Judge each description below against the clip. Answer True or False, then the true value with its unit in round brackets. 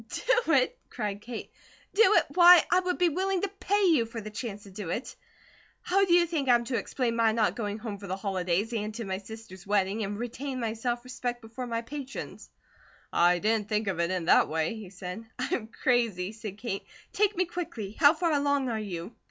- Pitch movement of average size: False (5.7 semitones)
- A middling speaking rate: False (215 wpm)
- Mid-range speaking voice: False (230 Hz)